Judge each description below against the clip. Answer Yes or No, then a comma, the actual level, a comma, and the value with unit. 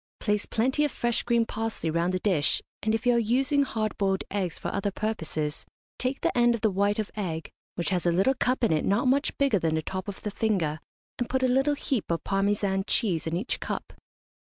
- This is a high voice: Yes, high, 210 Hz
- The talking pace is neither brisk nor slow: No, fast, 225 wpm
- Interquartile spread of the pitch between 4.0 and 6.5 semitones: Yes, average, 4.6 semitones